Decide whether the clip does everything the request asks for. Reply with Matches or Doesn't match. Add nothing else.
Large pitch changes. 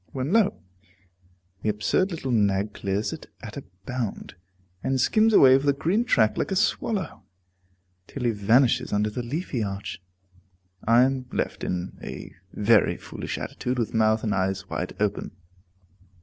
Doesn't match